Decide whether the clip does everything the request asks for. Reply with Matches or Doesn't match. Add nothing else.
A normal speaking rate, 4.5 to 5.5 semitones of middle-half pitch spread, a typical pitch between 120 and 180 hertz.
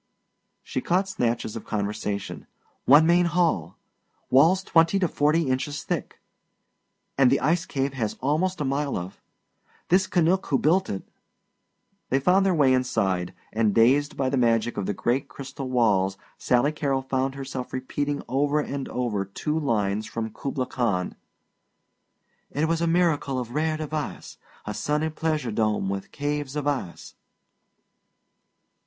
Matches